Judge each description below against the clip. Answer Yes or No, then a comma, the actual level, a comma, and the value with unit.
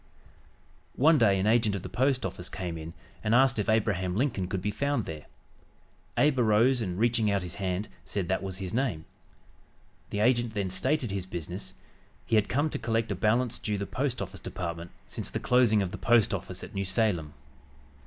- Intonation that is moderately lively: Yes, average, 4.3 semitones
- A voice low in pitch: Yes, low, 105 Hz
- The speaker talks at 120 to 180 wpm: No, average, 200 wpm